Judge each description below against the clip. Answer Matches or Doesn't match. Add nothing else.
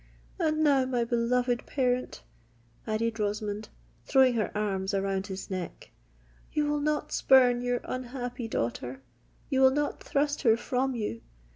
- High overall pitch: Matches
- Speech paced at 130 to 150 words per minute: Matches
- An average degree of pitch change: Matches